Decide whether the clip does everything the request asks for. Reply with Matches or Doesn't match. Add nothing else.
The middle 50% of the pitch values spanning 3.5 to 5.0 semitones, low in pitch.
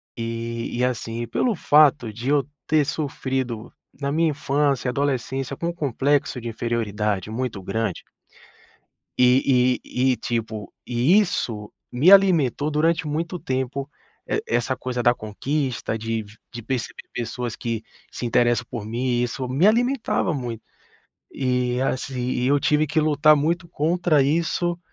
Matches